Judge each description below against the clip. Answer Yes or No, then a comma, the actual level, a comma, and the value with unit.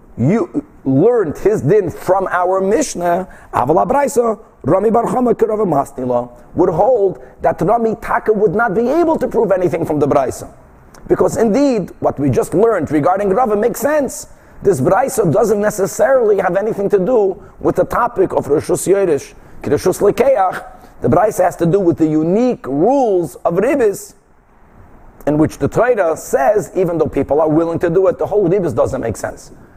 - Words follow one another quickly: No, average, 165 wpm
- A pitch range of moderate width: No, wide, 6.1 semitones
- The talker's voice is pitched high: Yes, high, 200 Hz